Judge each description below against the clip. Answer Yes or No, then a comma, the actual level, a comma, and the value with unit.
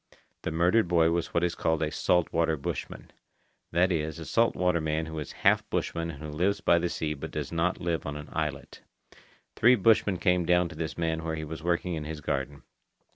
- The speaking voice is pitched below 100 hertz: Yes, very low, 85 Hz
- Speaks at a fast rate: Yes, fast, 215 wpm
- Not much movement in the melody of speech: Yes, narrow, 2.1 semitones